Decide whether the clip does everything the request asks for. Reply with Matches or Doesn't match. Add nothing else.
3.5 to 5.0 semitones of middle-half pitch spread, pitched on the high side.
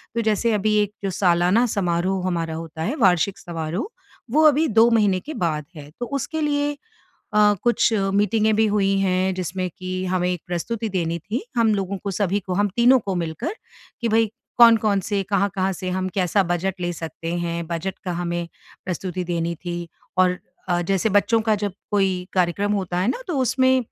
Matches